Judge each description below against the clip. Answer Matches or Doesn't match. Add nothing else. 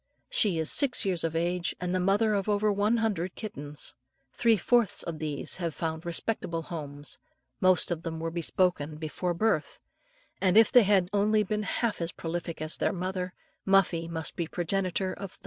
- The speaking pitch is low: Doesn't match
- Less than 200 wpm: Matches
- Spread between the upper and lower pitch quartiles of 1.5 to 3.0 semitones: Doesn't match